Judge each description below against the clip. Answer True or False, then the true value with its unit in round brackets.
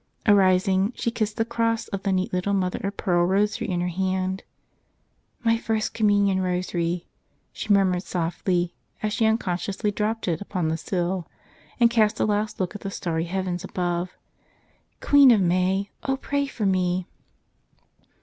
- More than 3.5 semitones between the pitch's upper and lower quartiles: False (2.9 semitones)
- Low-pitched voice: False (190 Hz)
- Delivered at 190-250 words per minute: False (160 wpm)